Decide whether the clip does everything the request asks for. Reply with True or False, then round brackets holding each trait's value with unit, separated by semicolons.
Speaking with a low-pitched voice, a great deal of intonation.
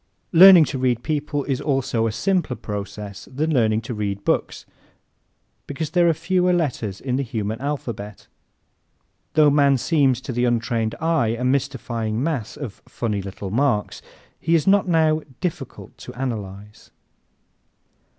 True (130 Hz; 5.8 semitones)